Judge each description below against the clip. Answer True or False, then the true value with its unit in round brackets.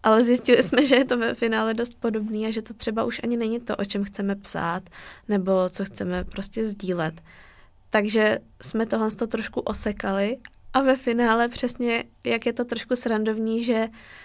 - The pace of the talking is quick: True (185 wpm)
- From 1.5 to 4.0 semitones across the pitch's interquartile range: True (2.6 semitones)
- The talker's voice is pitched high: True (225 Hz)